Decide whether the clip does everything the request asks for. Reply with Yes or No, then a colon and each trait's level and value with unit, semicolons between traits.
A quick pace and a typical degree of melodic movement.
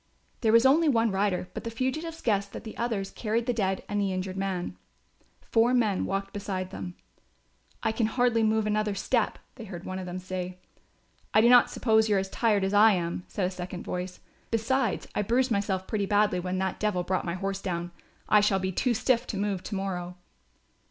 Yes: fast, 210 wpm; average, 3.3 semitones